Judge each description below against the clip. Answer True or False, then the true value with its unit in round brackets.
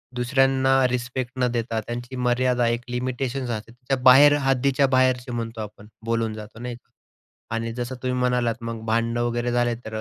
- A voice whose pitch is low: True (120 Hz)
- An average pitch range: False (1.8 semitones)